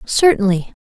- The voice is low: No, high, 230 Hz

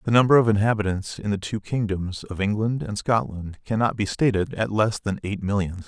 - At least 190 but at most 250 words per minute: Yes, fast, 205 wpm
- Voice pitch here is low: Yes, low, 105 Hz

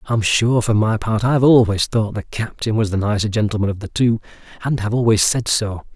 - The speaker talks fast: Yes, fast, 210 wpm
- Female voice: No, male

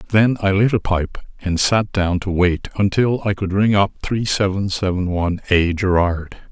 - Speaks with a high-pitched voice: No, very low, 95 Hz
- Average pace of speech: Yes, average, 195 wpm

